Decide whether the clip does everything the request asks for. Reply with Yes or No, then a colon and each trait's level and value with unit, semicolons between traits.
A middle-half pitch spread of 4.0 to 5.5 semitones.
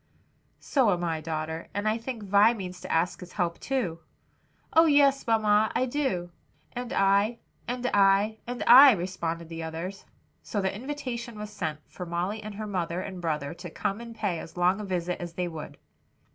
Yes: average, 4.8 semitones